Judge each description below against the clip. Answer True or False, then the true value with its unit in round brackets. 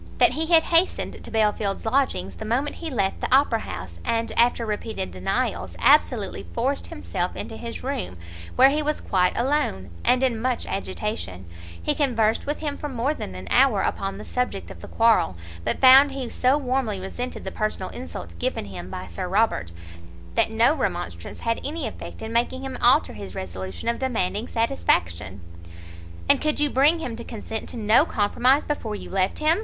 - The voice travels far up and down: True (6.6 semitones)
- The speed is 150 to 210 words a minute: True (185 wpm)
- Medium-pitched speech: False (225 Hz)